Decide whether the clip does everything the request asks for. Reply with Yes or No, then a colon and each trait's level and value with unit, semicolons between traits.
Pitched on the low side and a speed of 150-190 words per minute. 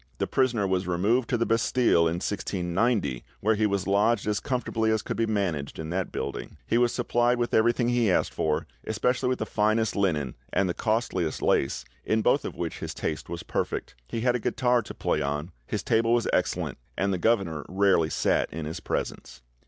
No: low, 105 Hz; average, 200 wpm